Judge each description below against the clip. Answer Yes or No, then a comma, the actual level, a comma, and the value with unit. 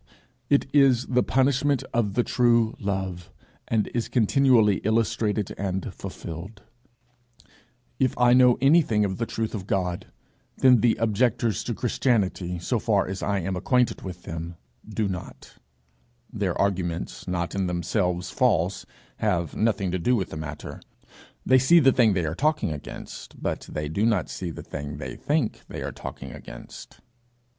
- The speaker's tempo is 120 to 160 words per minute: Yes, average, 155 wpm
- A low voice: Yes, low, 105 Hz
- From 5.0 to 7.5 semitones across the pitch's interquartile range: Yes, average, 5.3 semitones